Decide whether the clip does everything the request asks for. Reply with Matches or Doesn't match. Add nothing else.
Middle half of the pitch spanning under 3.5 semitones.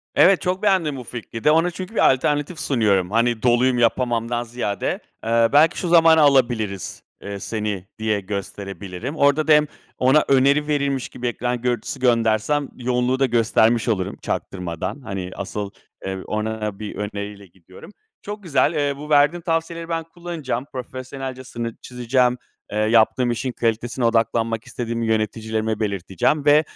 Doesn't match